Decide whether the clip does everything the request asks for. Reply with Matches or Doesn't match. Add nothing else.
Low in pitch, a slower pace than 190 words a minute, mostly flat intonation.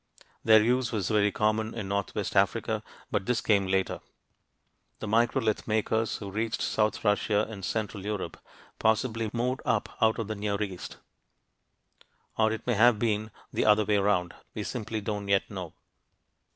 Matches